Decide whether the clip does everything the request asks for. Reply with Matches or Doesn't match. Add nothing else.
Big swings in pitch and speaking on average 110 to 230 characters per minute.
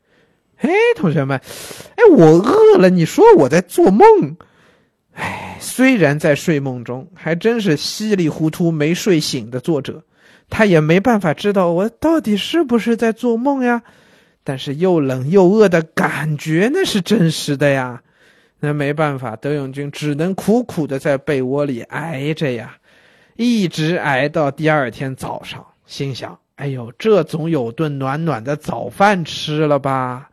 Matches